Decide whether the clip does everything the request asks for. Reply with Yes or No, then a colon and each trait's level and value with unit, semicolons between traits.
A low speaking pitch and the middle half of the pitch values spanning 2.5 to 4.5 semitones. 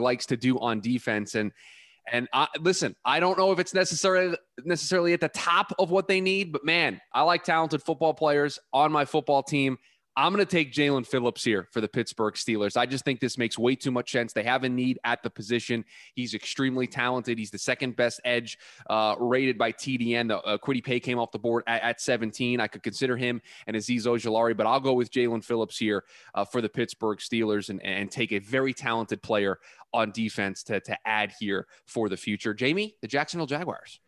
Yes: low, 125 Hz; average, 4.0 semitones